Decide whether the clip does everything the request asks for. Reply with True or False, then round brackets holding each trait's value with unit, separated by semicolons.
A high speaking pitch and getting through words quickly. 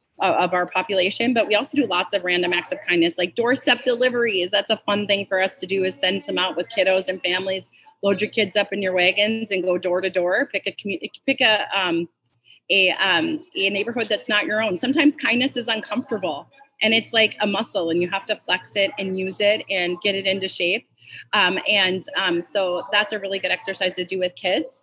True (195 Hz; 225 wpm)